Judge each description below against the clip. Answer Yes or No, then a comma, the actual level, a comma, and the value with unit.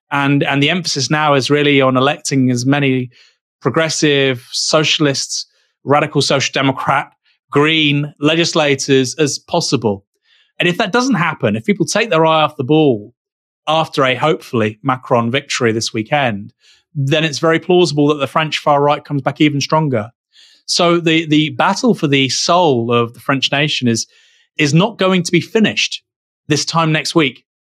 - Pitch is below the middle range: No, medium, 150 Hz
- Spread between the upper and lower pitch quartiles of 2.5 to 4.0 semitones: Yes, average, 3.1 semitones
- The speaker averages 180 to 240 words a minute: No, average, 160 wpm